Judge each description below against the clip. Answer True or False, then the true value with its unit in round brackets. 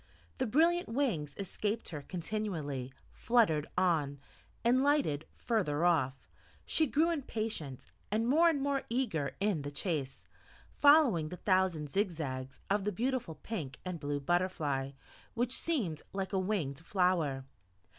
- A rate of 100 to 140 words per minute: True (135 wpm)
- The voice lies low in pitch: False (185 Hz)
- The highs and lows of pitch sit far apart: True (7.8 semitones)